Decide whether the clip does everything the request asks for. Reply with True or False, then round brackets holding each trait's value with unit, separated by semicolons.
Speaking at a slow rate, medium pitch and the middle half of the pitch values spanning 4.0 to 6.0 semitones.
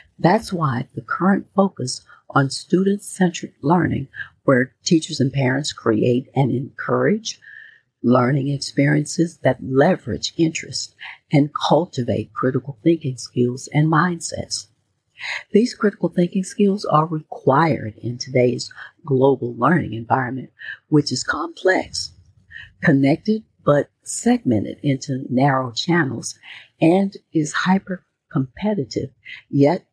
True (105 wpm; 145 Hz; 5.3 semitones)